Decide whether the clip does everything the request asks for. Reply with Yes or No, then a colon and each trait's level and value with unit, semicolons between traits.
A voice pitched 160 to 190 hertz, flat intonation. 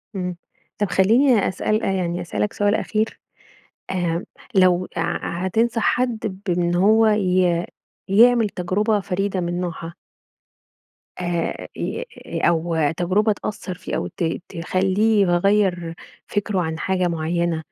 No: medium, 185 Hz; average, 3.2 semitones